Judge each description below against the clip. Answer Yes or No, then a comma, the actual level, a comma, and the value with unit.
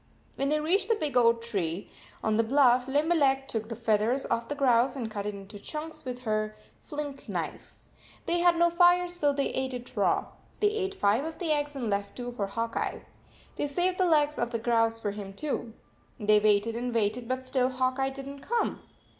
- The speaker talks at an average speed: No, fast, 215 wpm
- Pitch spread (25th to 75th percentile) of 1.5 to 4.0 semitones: No, average, 4.8 semitones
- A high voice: Yes, very high, 255 Hz